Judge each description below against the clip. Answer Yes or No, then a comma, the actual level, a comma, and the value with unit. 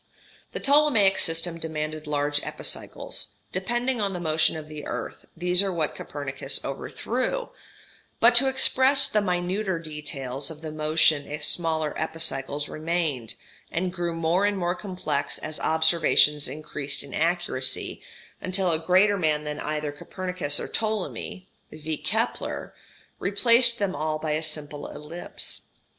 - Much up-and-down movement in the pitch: No, average, 4.0 semitones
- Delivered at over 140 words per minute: No, slow, 135 wpm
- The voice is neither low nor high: Yes, medium, 165 Hz